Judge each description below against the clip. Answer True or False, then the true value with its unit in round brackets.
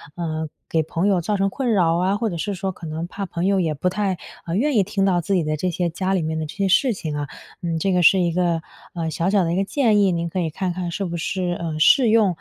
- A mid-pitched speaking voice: True (180 Hz)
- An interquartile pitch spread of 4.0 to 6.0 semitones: False (2.8 semitones)